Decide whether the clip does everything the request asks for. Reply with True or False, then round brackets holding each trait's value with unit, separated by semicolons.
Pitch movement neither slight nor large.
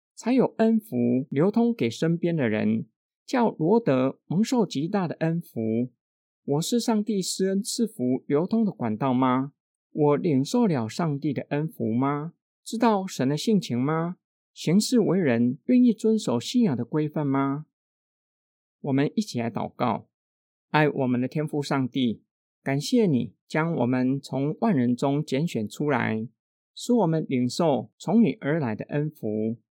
False (8.0 semitones)